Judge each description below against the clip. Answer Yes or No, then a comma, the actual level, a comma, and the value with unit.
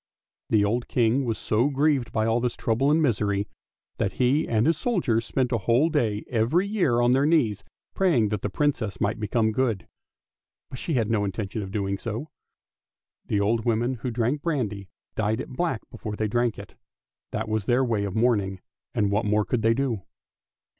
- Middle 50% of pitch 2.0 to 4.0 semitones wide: Yes, average, 3.7 semitones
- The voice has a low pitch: Yes, low, 115 Hz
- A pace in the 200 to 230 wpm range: No, average, 190 wpm